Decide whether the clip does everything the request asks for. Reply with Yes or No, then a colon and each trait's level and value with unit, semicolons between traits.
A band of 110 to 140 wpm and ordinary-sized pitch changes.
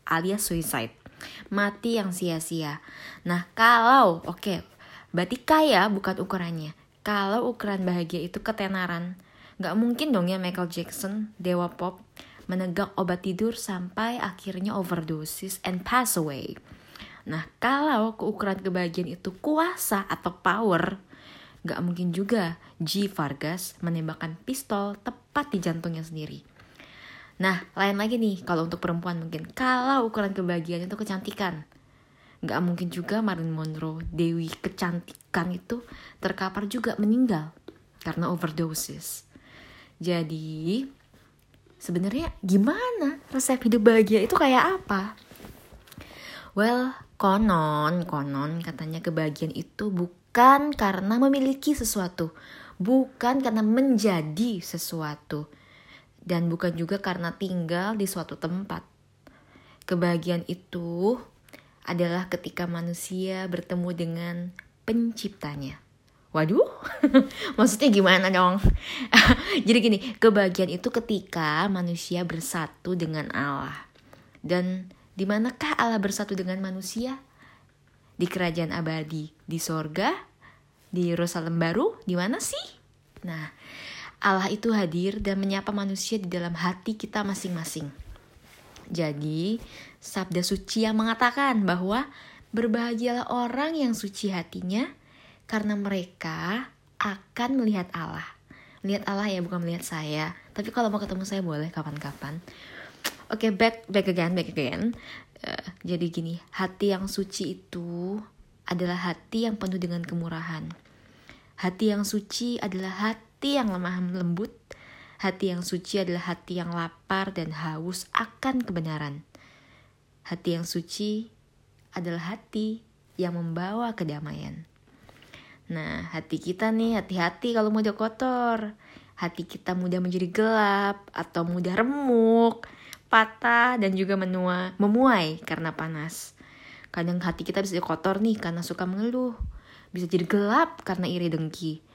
Yes: average, 120 wpm; average, 4.2 semitones